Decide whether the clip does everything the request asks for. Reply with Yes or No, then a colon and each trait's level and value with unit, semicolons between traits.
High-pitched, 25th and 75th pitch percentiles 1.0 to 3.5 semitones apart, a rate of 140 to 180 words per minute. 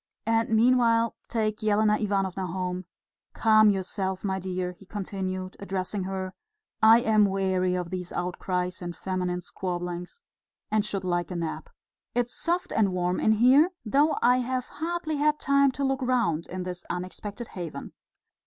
No: high, 195 Hz; average, 4.2 semitones; average, 155 wpm